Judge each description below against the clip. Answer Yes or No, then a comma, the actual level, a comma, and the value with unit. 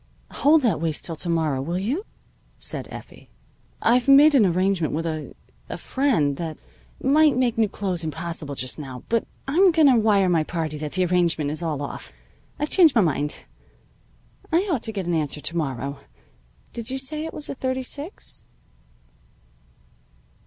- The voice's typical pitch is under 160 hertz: No, medium, 185 Hz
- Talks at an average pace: Yes, average, 170 wpm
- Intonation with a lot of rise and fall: Yes, wide, 9.0 semitones